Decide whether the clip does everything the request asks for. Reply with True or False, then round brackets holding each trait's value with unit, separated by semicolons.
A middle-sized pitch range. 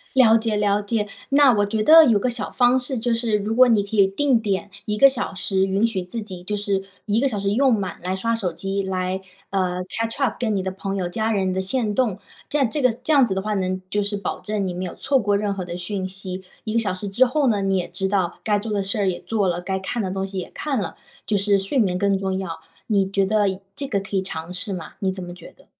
True (3.0 semitones)